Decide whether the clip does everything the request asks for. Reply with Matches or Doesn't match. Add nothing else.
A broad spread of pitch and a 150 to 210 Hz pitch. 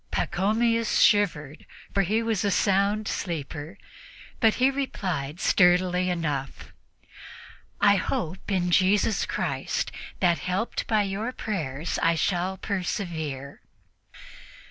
Doesn't match